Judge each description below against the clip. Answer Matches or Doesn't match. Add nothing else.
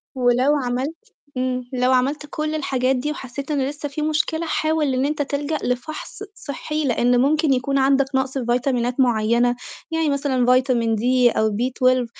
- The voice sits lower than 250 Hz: Doesn't match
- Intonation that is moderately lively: Matches